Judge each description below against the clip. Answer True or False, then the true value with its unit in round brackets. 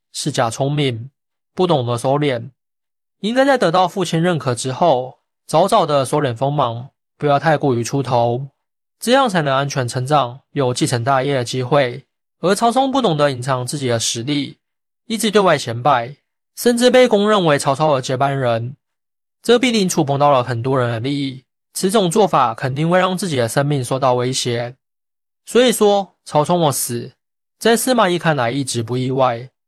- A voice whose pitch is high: False (140 Hz)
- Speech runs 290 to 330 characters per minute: False (260 characters per minute)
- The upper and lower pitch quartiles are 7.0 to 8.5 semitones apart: False (5.7 semitones)